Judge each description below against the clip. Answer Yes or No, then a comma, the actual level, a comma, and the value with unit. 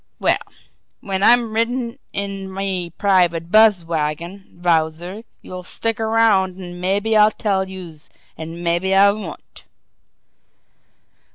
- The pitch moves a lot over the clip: No, average, 3.4 semitones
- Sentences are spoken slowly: Yes, slow, 115 wpm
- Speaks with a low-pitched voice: No, high, 190 Hz